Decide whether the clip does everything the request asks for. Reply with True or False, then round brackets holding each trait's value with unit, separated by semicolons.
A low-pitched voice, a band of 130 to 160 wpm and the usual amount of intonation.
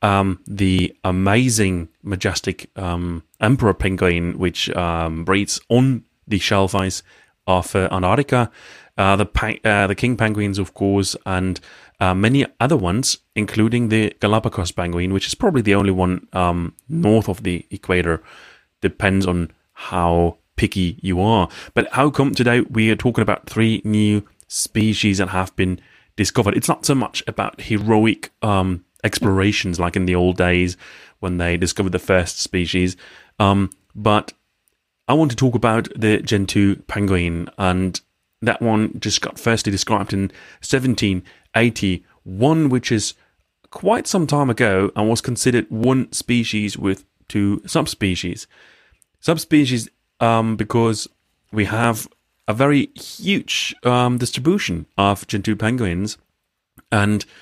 True (100 Hz; 135 wpm; 3.4 semitones)